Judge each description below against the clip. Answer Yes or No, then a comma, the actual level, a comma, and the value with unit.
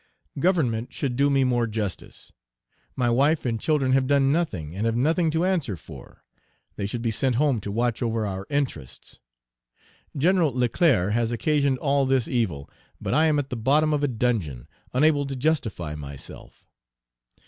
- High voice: No, low, 125 Hz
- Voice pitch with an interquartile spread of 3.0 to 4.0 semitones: No, average, 4.5 semitones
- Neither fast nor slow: Yes, average, 170 wpm